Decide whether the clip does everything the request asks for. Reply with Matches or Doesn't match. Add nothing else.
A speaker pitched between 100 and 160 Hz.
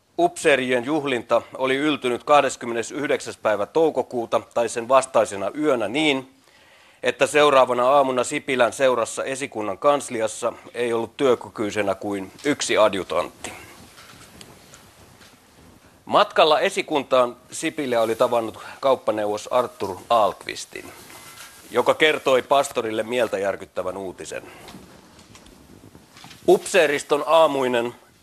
Matches